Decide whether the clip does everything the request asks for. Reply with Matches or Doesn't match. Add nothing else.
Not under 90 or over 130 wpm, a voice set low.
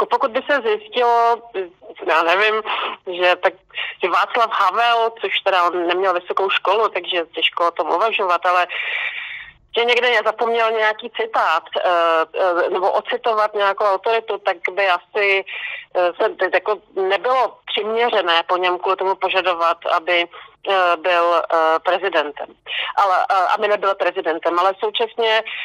Doesn't match